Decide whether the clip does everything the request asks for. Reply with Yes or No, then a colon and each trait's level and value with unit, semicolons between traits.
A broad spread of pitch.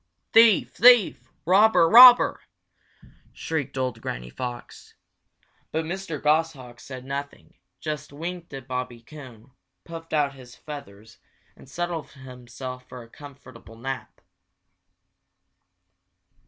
No: average, 4.5 semitones